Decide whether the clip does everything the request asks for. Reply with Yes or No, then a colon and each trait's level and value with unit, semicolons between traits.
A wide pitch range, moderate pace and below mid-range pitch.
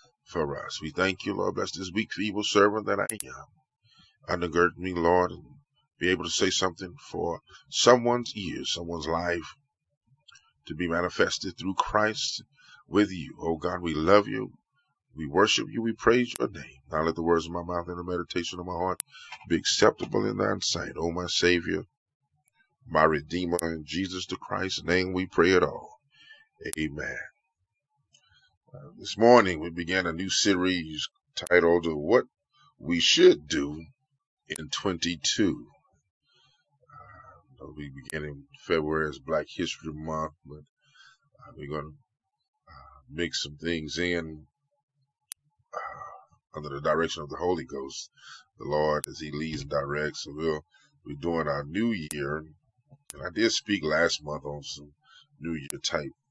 Yes: wide, 6.9 semitones; average, 155 wpm; very low, 90 Hz